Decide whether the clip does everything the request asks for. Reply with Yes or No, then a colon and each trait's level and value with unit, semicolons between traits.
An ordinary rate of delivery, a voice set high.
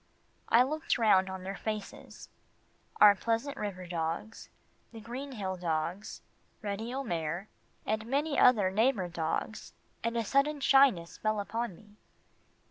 No: slow, 130 wpm; high, 215 Hz